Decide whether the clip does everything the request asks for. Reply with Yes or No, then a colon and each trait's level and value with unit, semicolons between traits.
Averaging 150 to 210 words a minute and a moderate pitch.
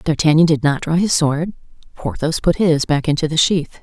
Yes: fast, 205 wpm; medium, 160 Hz